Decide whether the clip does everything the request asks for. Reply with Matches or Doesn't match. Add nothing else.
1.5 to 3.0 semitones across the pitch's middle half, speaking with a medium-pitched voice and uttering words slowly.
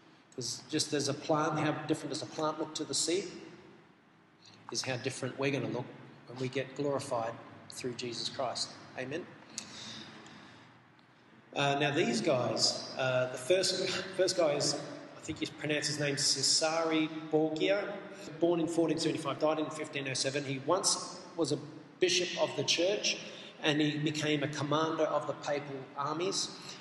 Doesn't match